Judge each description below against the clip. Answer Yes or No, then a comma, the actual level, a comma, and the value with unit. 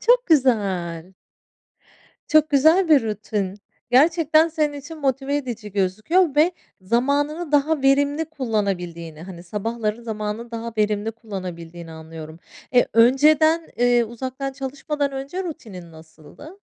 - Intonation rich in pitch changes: Yes, wide, 6.8 semitones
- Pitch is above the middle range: Yes, high, 240 Hz